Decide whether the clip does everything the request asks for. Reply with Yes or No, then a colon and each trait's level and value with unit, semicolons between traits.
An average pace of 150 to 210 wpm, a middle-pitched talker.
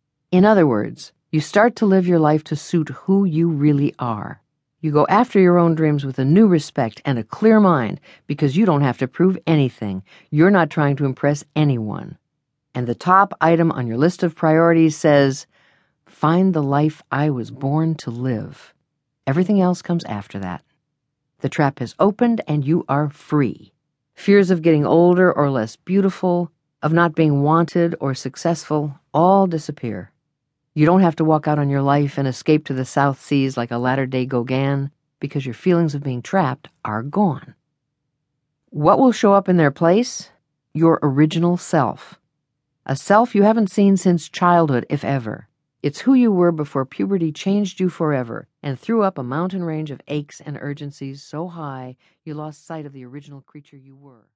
Yes: average, 180 wpm; medium, 150 Hz